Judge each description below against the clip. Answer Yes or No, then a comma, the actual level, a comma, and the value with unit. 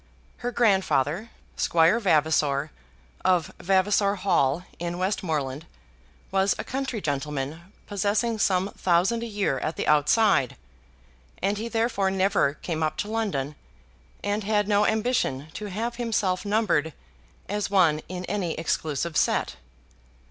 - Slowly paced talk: Yes, slow, 125 wpm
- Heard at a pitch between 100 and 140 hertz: No, high, 190 Hz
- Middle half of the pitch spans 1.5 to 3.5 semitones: No, average, 4.8 semitones